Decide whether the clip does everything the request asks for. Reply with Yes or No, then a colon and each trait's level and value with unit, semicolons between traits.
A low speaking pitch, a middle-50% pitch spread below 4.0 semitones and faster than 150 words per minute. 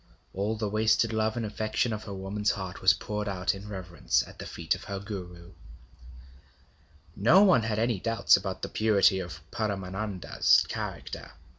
Yes: low, 105 Hz; narrow, 2.4 semitones; average, 165 wpm